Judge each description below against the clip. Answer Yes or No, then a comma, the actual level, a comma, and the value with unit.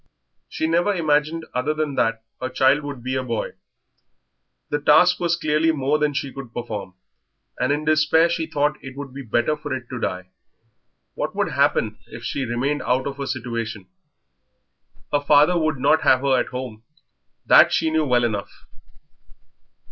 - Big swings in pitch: No, average, 3.3 semitones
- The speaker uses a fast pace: No, average, 170 wpm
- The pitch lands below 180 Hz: Yes, medium, 140 Hz